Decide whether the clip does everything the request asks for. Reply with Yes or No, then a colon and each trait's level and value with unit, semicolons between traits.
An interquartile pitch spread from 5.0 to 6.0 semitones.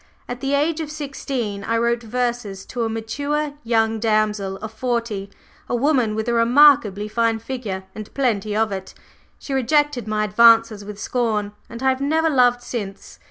No: average, 3.5 semitones